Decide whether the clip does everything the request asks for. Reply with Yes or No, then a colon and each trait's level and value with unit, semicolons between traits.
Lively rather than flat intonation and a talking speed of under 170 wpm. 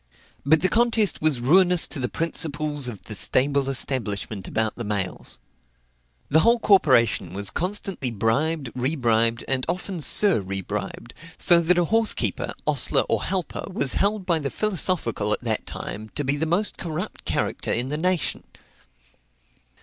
Yes: wide, 7.5 semitones; average, 155 wpm